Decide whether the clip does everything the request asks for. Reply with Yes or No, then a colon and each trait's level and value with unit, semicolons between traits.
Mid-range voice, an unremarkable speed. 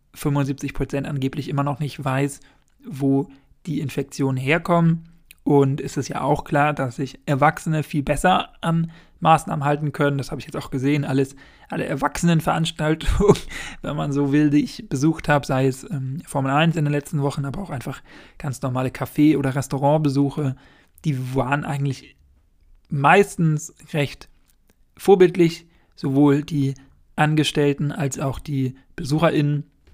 Yes: medium, 145 Hz; average, 145 wpm